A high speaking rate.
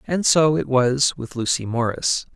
No: average, 180 wpm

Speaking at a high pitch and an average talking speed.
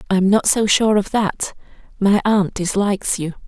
Yes: high, 200 Hz; average, 155 wpm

